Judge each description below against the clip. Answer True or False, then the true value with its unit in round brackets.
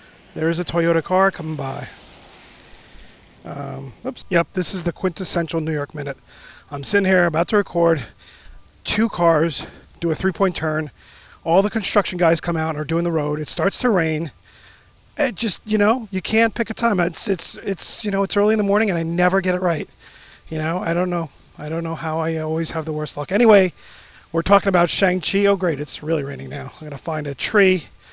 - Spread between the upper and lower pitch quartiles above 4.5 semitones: False (3.8 semitones)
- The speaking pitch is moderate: True (170 Hz)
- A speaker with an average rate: False (215 wpm)